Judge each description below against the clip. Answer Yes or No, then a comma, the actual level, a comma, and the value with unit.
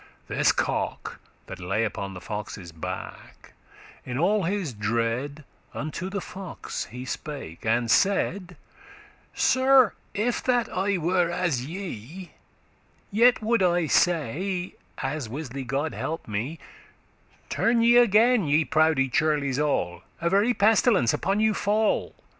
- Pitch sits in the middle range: Yes, medium, 165 Hz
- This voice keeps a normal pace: No, slow, 130 wpm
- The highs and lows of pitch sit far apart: Yes, wide, 7.7 semitones